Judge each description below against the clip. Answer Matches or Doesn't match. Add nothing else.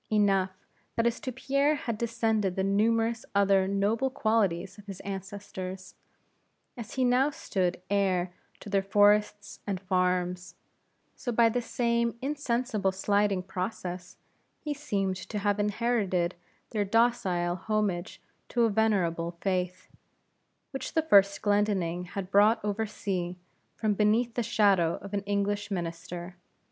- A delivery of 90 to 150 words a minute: Matches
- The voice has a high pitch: Matches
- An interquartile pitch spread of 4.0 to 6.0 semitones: Doesn't match